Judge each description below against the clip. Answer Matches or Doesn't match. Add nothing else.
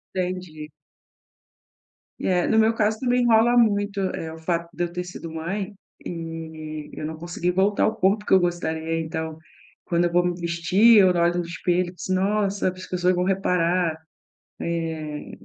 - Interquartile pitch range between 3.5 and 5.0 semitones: Doesn't match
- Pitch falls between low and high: Matches